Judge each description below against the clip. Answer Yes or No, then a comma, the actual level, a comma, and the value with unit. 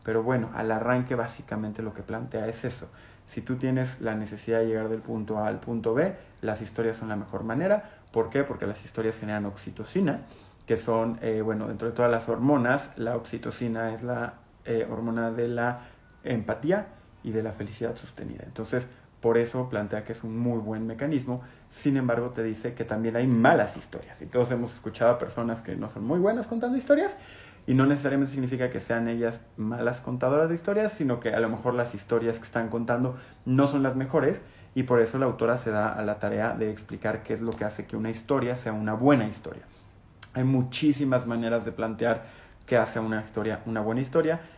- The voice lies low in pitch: Yes, low, 115 Hz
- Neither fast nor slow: No, fast, 205 wpm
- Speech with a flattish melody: Yes, narrow, 2.3 semitones